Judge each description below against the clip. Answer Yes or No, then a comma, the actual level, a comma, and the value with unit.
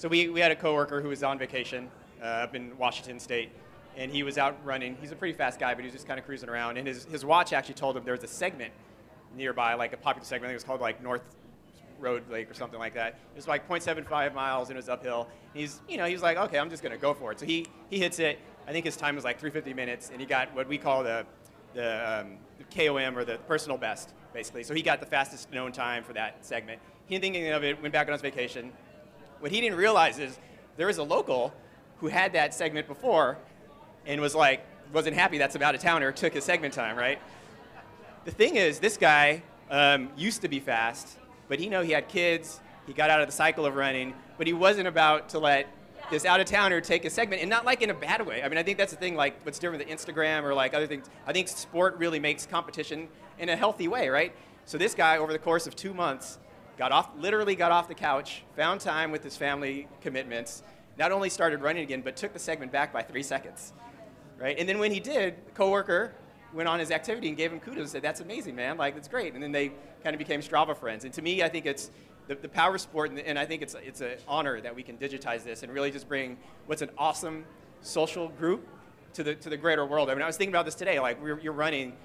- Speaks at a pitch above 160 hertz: No, medium, 150 Hz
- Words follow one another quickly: Yes, fast, 255 wpm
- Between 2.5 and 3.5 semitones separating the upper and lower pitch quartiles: No, average, 4.1 semitones